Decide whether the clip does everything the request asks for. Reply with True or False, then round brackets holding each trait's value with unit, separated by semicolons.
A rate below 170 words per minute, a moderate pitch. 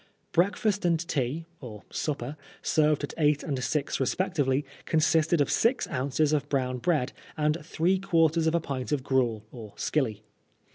True (155 wpm; 150 Hz)